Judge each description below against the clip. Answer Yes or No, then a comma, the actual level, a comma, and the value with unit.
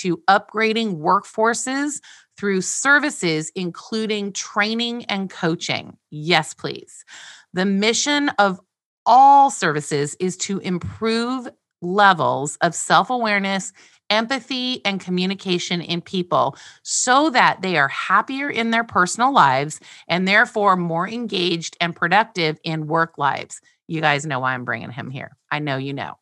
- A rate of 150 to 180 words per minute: No, slow, 135 wpm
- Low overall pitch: No, high, 190 Hz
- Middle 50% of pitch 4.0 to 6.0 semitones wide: Yes, average, 5.2 semitones